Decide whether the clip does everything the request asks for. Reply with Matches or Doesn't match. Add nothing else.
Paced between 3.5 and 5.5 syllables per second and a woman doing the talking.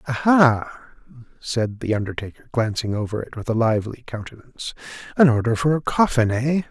Doesn't match